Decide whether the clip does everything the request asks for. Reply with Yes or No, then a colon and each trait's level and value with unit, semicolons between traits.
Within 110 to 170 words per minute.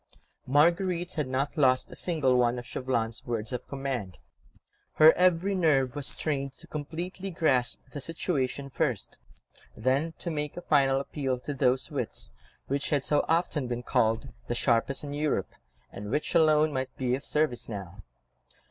Yes: average, 160 wpm